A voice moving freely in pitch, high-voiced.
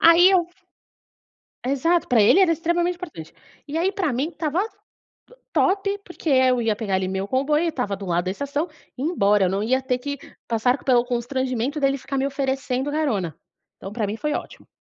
Yes: wide, 6.1 semitones; very high, 265 Hz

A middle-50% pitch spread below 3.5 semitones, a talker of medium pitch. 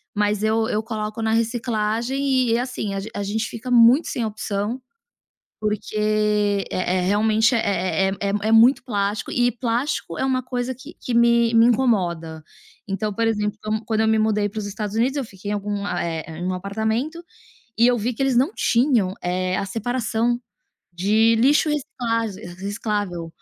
No: average, 2.8 semitones; high, 220 Hz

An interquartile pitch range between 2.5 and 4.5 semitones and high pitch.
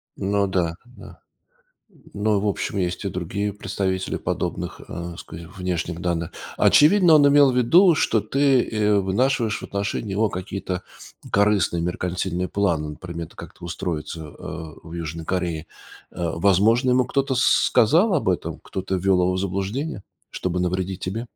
No: average, 4.1 semitones; very low, 95 Hz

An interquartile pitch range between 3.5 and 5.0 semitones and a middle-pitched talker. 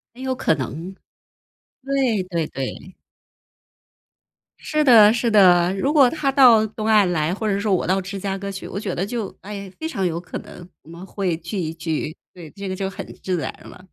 No: average, 3.9 semitones; high, 195 Hz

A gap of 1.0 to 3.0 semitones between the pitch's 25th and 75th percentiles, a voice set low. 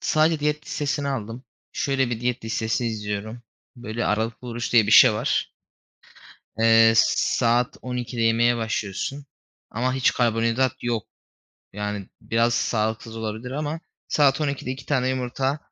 Yes: average, 2.7 semitones; low, 120 Hz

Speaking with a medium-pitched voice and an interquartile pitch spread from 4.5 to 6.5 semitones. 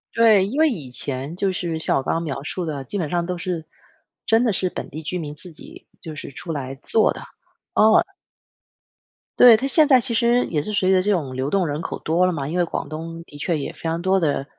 Yes: medium, 170 Hz; average, 5.0 semitones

